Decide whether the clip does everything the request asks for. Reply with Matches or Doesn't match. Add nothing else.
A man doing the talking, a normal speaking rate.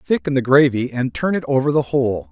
Doesn't match